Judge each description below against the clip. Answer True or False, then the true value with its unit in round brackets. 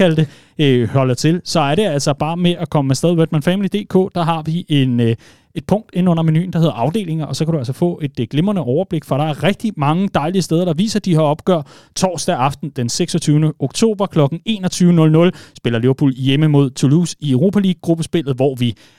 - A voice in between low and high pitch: True (160 Hz)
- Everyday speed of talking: True (200 wpm)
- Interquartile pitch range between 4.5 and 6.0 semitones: False (3.9 semitones)